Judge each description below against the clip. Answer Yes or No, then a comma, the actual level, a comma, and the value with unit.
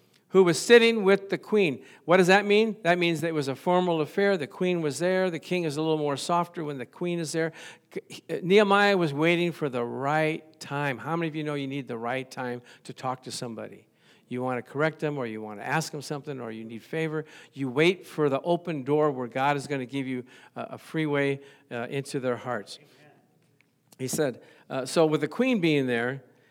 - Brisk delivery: Yes, fast, 220 wpm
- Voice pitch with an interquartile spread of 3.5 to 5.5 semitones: Yes, average, 4.7 semitones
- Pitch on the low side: No, medium, 150 Hz